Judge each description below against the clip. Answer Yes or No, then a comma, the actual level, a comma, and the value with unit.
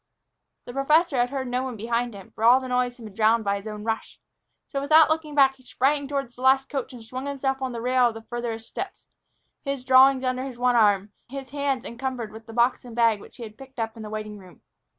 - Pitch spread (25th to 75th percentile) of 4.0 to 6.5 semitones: No, average, 3.0 semitones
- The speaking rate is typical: No, fast, 245 wpm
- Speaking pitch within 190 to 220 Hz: No, very high, 250 Hz